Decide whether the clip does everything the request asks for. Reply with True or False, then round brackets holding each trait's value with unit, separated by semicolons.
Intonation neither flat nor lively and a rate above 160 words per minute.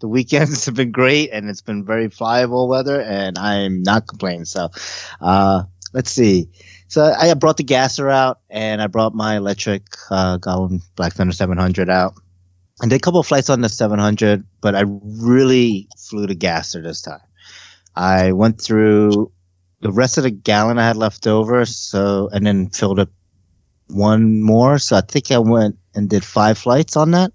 True (4.5 semitones; 180 wpm)